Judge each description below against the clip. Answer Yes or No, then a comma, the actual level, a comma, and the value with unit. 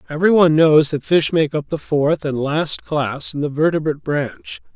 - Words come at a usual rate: Yes, average, 190 wpm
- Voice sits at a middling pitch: Yes, medium, 150 Hz